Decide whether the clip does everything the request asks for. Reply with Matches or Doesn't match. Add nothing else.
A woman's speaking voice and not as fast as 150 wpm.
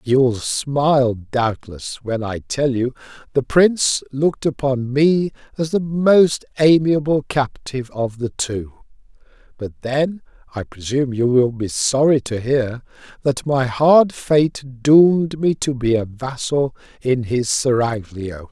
Doesn't match